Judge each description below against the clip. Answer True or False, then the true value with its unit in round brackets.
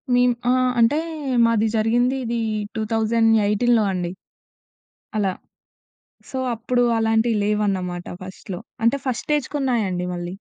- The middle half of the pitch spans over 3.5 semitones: False (3.0 semitones)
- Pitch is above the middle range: True (225 Hz)